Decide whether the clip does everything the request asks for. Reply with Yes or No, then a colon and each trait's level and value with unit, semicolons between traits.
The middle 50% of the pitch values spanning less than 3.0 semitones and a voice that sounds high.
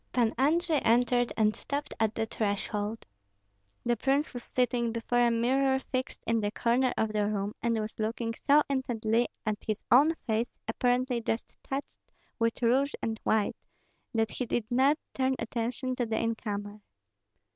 Yes: narrow, 2.6 semitones; high, 235 Hz